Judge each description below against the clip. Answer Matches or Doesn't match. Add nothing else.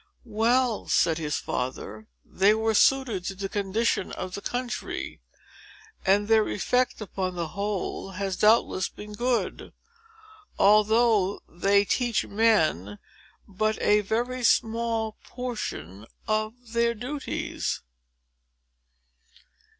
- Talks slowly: Matches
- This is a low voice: Doesn't match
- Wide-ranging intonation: Doesn't match